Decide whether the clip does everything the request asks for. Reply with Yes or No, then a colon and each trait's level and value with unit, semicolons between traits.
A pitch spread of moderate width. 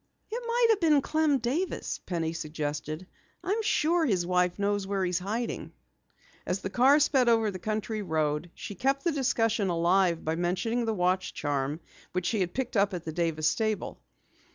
No: wide, 6.4 semitones